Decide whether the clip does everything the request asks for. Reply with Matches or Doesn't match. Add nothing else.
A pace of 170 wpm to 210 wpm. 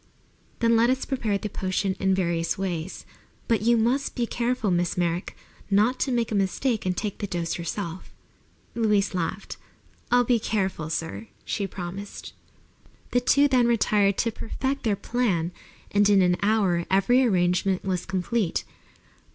Doesn't match